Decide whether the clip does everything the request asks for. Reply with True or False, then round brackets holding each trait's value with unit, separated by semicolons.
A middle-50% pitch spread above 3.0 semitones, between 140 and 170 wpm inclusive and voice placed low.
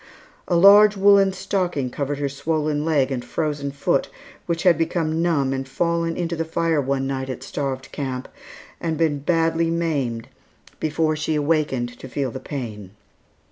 False (3.7 semitones; 160 wpm; 155 Hz)